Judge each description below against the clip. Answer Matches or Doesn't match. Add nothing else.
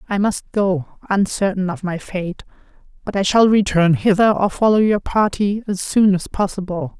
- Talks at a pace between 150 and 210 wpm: Matches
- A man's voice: Doesn't match